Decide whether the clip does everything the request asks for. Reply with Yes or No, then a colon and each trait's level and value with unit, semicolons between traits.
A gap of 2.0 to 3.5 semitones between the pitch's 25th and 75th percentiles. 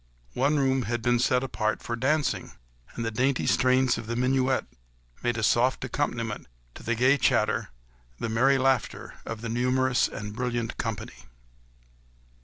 Yes: narrow, 2.4 semitones